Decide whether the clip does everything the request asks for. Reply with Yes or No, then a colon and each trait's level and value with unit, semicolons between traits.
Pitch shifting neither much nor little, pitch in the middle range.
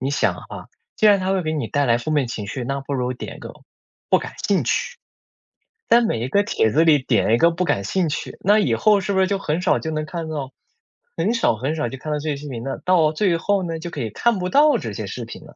No: wide, 6.0 semitones; medium, 155 Hz